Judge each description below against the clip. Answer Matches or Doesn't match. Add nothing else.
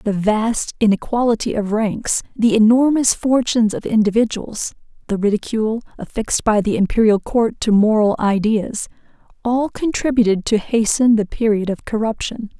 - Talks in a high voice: Matches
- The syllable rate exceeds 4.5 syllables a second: Matches